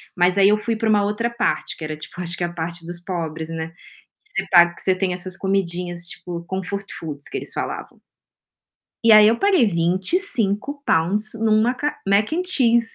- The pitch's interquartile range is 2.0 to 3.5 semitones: No, average, 4.4 semitones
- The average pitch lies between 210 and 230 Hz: No, high, 195 Hz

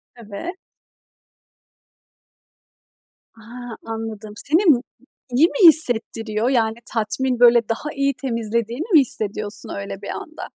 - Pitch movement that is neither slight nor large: Yes, average, 3.9 semitones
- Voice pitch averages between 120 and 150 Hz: No, high, 235 Hz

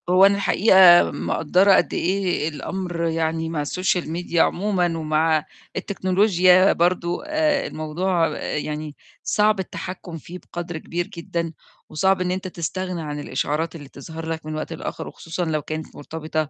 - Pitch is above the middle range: No, medium, 170 Hz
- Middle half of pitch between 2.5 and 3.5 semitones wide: Yes, average, 2.8 semitones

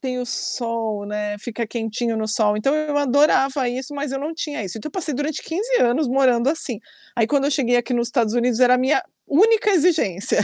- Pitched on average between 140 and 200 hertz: No, very high, 250 Hz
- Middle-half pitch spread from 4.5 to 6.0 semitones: No, average, 4.1 semitones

